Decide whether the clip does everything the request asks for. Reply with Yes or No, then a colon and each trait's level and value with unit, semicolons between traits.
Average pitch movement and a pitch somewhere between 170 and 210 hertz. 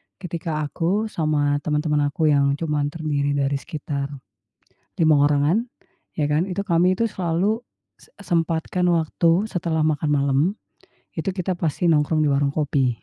No: average, 3.0 semitones; medium, 155 Hz